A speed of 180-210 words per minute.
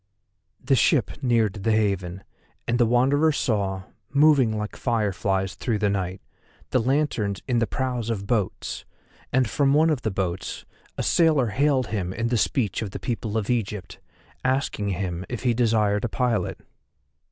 No: average, 165 wpm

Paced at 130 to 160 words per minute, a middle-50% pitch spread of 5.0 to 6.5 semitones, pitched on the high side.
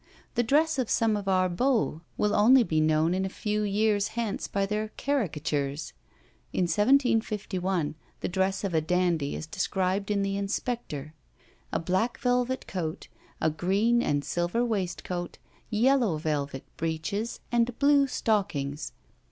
Yes: average, 145 wpm; wide, 5.6 semitones; high, 195 Hz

